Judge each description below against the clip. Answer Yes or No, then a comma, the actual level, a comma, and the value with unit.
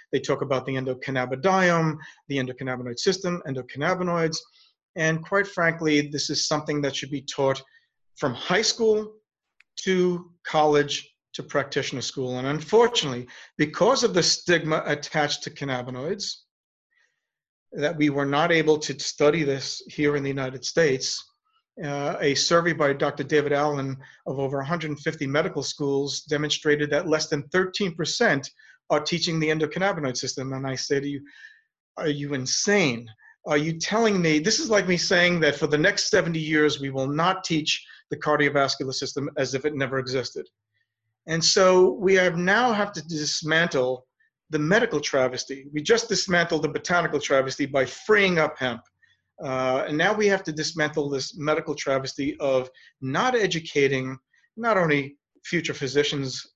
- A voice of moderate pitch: Yes, medium, 150 Hz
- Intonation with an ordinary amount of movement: Yes, average, 3.9 semitones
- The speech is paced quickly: No, average, 155 wpm